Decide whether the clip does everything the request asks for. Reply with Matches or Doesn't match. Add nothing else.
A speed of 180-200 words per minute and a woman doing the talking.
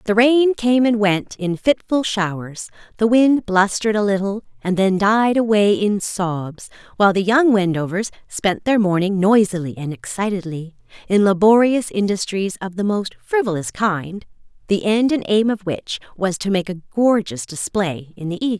Doesn't match